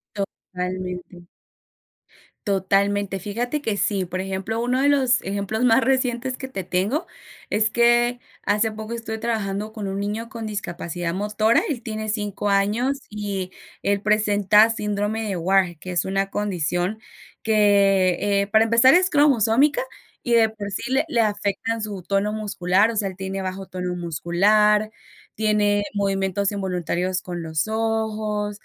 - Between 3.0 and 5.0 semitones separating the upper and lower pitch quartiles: No, narrow, 2.6 semitones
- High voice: Yes, high, 205 Hz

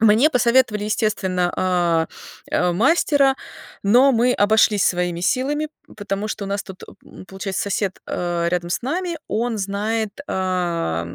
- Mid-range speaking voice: No, high, 205 Hz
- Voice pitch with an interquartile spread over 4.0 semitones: Yes, average, 4.8 semitones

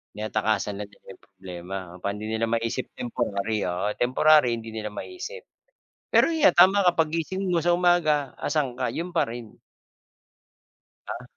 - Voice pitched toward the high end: No, low, 120 Hz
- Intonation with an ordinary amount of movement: No, wide, 8.3 semitones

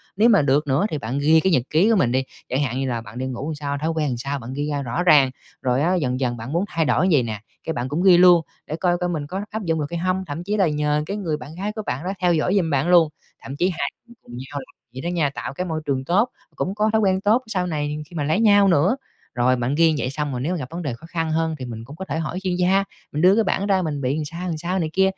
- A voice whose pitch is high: No, medium, 160 Hz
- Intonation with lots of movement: No, average, 4.7 semitones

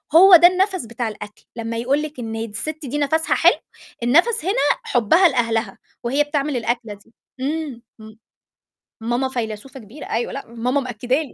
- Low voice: No, very high, 255 Hz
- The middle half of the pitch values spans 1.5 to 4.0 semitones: No, average, 4.8 semitones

